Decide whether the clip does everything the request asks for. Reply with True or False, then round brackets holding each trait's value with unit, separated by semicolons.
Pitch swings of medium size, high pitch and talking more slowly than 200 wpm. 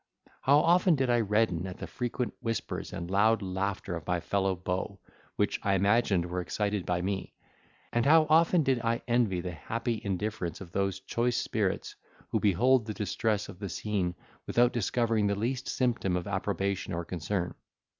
False (4.3 semitones; 100 Hz; 175 wpm)